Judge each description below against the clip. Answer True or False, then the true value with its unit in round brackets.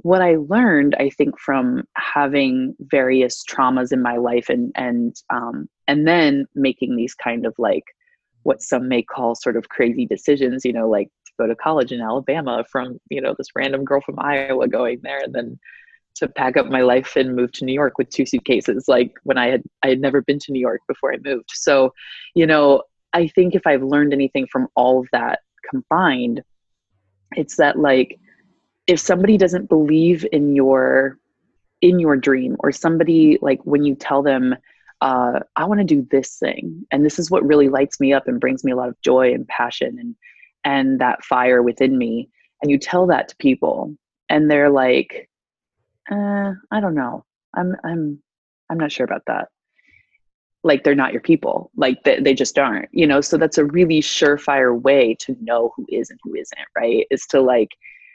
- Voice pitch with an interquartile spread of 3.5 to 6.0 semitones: True (4.6 semitones)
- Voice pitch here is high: False (140 Hz)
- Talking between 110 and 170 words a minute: False (195 wpm)